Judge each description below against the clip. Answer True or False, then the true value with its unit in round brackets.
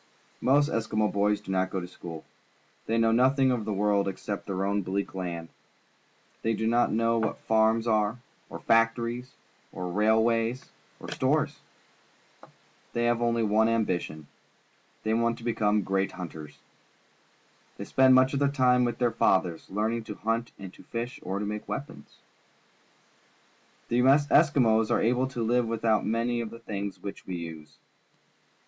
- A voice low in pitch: True (110 Hz)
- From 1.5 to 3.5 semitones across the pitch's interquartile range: True (3.0 semitones)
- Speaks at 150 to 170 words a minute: True (160 wpm)